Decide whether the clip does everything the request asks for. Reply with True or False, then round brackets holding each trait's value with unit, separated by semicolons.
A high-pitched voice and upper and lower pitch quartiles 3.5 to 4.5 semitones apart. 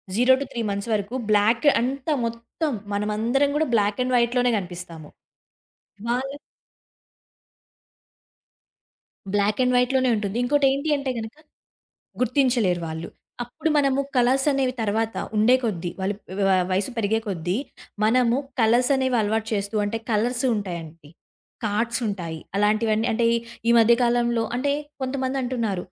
True (230 Hz; 3.8 semitones)